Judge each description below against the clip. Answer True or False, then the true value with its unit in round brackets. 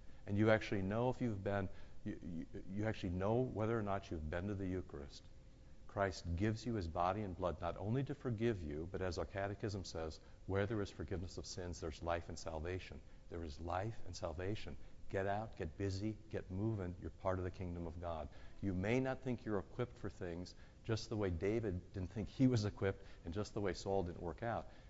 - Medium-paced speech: False (215 wpm)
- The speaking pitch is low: True (95 Hz)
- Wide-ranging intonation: False (3.8 semitones)